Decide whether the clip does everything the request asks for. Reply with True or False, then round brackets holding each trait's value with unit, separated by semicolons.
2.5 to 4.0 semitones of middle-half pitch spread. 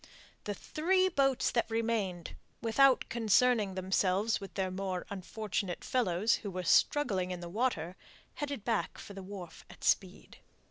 False (4.5 semitones)